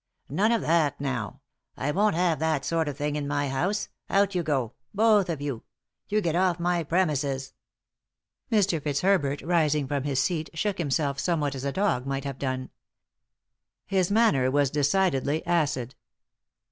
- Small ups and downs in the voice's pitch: No, average, 4.5 semitones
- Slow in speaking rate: No, average, 170 wpm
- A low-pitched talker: No, medium, 150 Hz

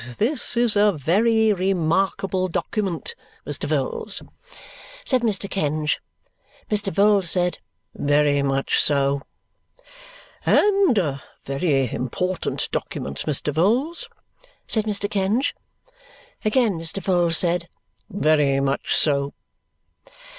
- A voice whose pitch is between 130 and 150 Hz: No, medium, 185 Hz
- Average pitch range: No, wide, 6.2 semitones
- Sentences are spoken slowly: Yes, slow, 105 wpm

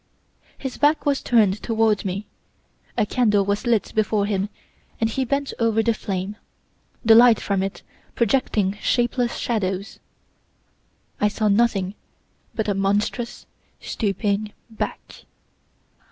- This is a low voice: No, high, 215 Hz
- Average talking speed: No, slow, 125 wpm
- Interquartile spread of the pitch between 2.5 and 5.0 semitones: Yes, average, 2.8 semitones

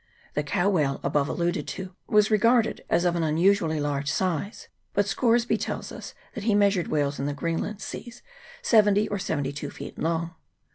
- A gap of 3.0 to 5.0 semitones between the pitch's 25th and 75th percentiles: No, wide, 5.4 semitones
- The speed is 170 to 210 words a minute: Yes, average, 180 wpm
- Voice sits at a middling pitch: Yes, medium, 175 Hz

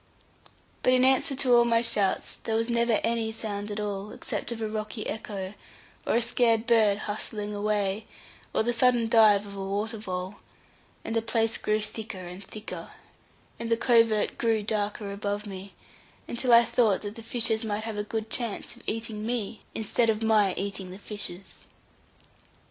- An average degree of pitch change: No, narrow, 2.0 semitones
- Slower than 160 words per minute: No, average, 175 wpm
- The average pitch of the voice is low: No, high, 220 Hz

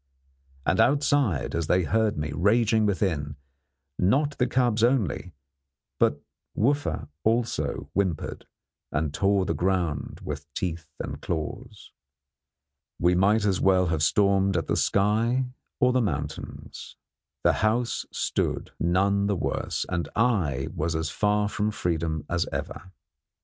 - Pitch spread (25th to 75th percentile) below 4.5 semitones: No, average, 4.9 semitones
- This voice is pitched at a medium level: No, very low, 95 Hz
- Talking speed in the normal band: No, slow, 130 wpm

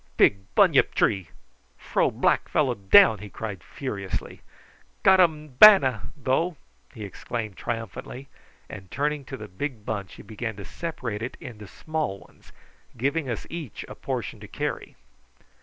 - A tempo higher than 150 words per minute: No, average, 145 wpm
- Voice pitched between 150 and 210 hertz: No, low, 120 Hz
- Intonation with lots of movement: Yes, wide, 6.2 semitones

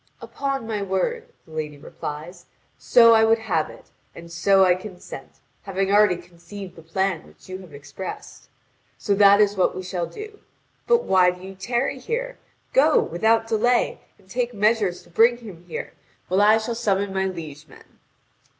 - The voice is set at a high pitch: Yes, high, 195 Hz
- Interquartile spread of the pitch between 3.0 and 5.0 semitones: Yes, average, 4.1 semitones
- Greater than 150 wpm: Yes, average, 175 wpm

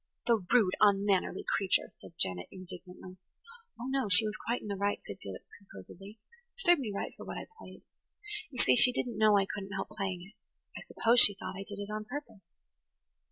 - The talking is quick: Yes, fast, 210 wpm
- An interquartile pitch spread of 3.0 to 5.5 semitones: No, narrow, 2.6 semitones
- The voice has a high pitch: Yes, high, 205 Hz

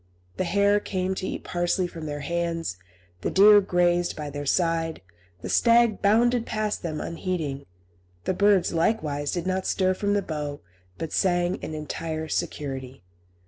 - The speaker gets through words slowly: No, average, 155 wpm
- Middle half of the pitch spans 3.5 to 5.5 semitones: Yes, average, 4.0 semitones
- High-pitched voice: No, medium, 175 Hz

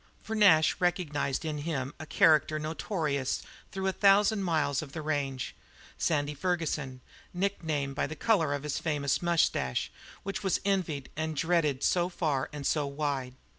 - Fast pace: No, average, 155 wpm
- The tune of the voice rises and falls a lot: No, average, 3.8 semitones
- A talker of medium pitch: Yes, medium, 155 Hz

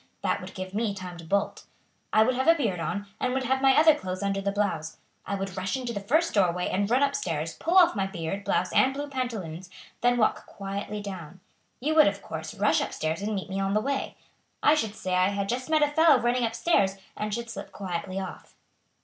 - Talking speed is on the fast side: Yes, fast, 240 wpm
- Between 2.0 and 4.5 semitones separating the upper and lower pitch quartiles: No, wide, 5.4 semitones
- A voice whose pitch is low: No, high, 200 Hz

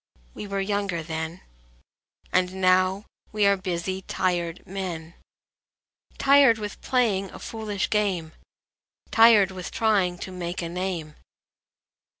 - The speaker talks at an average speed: No, slow, 120 wpm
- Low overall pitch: No, high, 190 Hz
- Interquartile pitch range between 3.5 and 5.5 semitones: No, average, 2.7 semitones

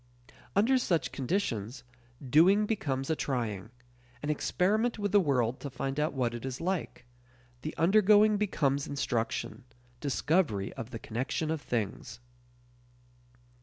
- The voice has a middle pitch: Yes, medium, 145 Hz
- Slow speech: Yes, slow, 130 wpm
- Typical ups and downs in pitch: No, wide, 7.4 semitones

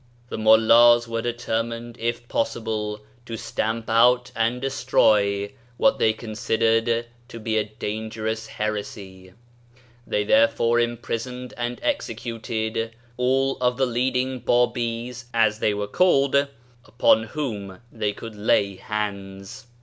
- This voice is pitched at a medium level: No, low, 115 Hz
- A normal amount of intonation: No, narrow, 2.0 semitones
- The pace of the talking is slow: Yes, slow, 120 wpm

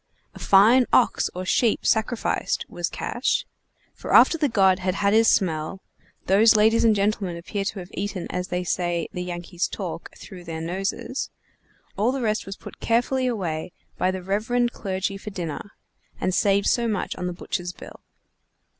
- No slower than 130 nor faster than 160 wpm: No, average, 170 wpm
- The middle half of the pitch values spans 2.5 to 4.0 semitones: Yes, average, 3.6 semitones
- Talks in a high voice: Yes, high, 195 Hz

